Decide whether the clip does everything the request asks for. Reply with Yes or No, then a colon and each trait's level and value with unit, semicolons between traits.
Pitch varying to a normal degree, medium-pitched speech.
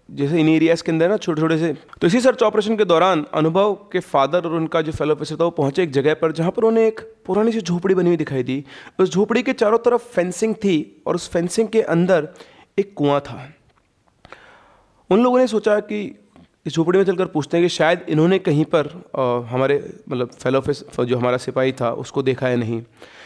No: wide, 6.2 semitones; medium, 165 Hz